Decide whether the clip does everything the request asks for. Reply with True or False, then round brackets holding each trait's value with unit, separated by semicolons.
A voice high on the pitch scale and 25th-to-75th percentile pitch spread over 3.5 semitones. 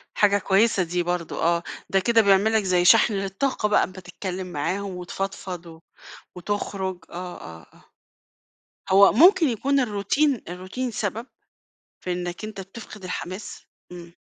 False (195 Hz; 3.2 semitones)